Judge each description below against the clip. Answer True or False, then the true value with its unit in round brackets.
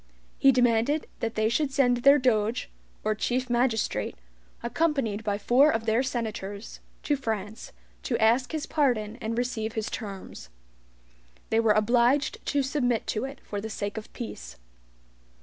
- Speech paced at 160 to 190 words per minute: False (150 wpm)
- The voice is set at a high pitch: True (235 Hz)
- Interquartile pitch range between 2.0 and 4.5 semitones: True (3.2 semitones)